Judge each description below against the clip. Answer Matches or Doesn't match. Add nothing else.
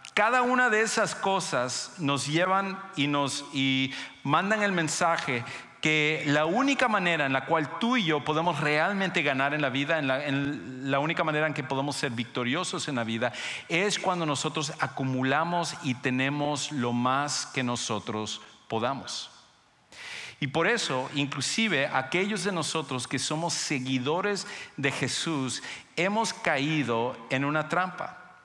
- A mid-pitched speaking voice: Matches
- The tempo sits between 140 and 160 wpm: Matches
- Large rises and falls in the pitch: Doesn't match